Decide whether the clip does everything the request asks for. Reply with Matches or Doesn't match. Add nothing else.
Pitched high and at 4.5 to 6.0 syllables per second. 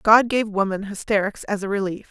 Matches